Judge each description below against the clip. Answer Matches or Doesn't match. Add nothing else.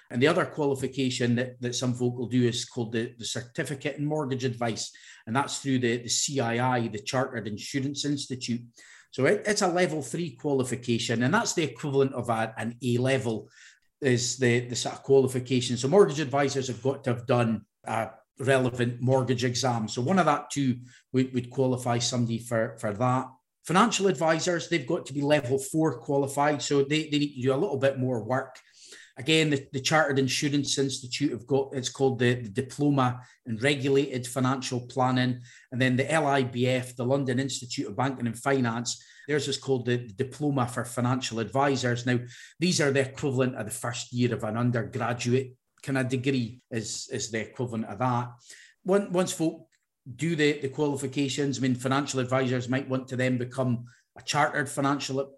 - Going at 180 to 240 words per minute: Matches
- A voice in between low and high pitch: Doesn't match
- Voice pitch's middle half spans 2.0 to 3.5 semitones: Matches